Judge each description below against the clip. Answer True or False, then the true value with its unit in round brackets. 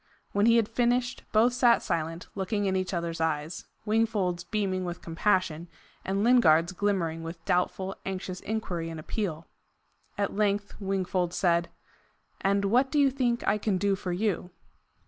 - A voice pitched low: False (195 Hz)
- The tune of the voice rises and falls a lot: False (3.7 semitones)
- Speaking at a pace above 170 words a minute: False (155 wpm)